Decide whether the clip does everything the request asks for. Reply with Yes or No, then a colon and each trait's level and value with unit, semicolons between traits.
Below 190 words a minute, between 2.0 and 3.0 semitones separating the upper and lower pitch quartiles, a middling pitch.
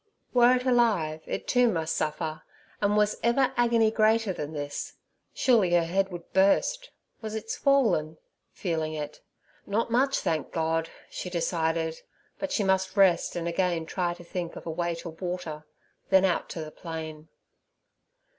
No: average, 155 wpm; average, 5.2 semitones; medium, 180 Hz